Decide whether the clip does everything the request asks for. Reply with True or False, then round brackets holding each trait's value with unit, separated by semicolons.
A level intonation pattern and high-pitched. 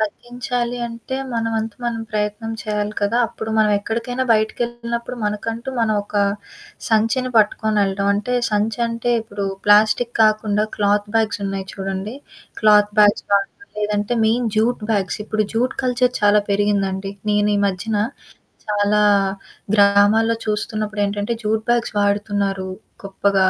True (2.0 semitones; 215 Hz)